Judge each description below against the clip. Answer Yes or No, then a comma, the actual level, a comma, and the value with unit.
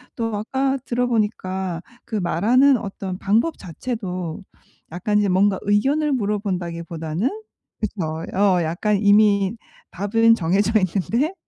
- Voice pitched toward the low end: No, high, 205 Hz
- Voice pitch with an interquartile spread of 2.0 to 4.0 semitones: Yes, average, 3.7 semitones